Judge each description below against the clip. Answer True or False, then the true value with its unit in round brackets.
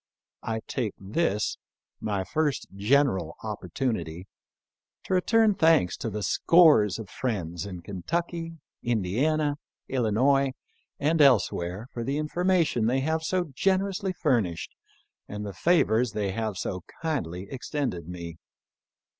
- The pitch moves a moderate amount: False (8.2 semitones)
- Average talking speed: False (120 wpm)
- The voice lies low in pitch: True (120 Hz)